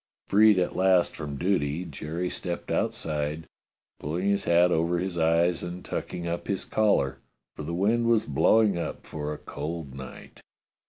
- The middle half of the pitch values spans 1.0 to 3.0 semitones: No, average, 3.4 semitones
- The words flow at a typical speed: Yes, average, 160 wpm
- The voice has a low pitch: Yes, very low, 85 Hz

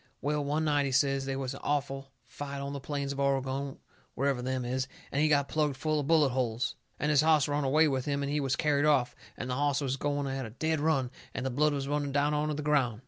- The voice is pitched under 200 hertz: Yes, medium, 140 Hz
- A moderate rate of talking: No, fast, 255 wpm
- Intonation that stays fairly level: Yes, narrow, 1.7 semitones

